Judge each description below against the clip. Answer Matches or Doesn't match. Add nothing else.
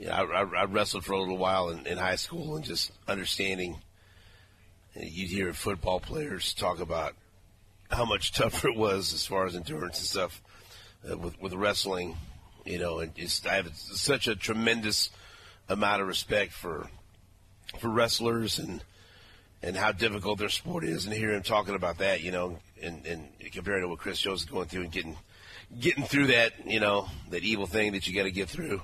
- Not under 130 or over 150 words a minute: Doesn't match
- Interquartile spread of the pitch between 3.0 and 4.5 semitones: Doesn't match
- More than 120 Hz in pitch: Doesn't match